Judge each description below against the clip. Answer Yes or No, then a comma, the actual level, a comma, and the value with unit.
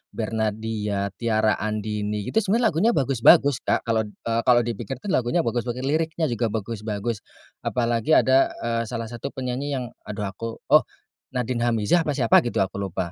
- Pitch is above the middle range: No, low, 115 Hz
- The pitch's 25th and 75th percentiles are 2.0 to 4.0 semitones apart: Yes, average, 3.5 semitones